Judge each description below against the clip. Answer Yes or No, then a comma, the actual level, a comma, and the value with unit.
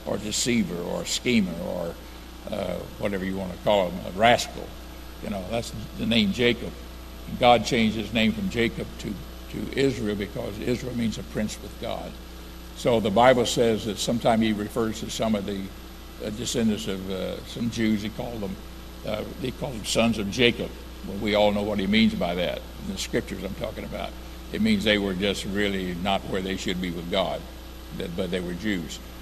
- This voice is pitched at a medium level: No, low, 105 Hz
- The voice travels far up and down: No, average, 4.8 semitones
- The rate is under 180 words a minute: No, average, 200 wpm